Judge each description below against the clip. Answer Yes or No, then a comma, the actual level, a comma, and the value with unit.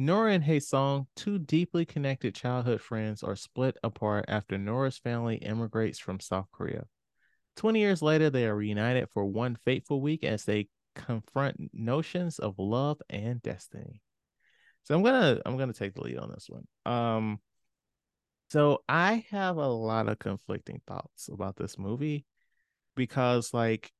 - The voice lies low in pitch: Yes, low, 120 Hz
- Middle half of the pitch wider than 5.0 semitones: Yes, wide, 5.4 semitones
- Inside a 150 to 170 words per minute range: Yes, average, 160 wpm